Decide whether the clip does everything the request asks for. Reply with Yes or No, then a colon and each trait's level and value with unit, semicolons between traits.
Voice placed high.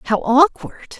Yes: very high, 270 Hz